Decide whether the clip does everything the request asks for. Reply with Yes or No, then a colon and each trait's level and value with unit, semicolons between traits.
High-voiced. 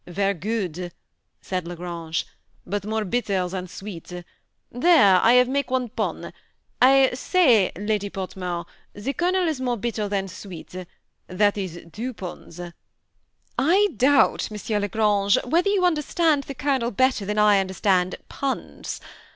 Yes: high, 210 Hz